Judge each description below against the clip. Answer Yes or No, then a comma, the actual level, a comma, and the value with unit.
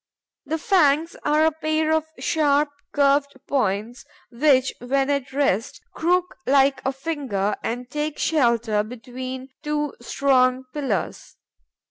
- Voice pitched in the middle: No, very high, 275 Hz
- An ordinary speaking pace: No, slow, 120 wpm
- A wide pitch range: No, average, 3.1 semitones